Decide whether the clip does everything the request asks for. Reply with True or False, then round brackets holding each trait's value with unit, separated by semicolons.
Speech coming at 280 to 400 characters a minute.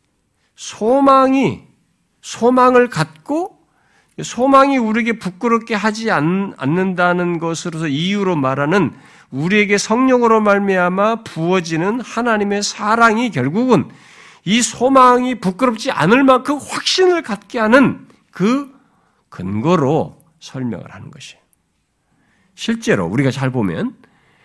False (250 characters per minute)